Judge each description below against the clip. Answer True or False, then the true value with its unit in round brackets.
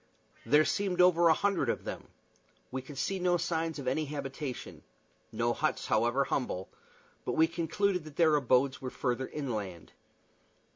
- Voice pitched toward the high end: False (150 Hz)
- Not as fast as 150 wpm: False (155 wpm)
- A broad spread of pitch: False (4.7 semitones)